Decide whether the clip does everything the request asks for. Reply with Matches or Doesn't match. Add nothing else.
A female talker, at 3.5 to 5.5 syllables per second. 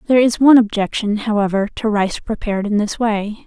Doesn't match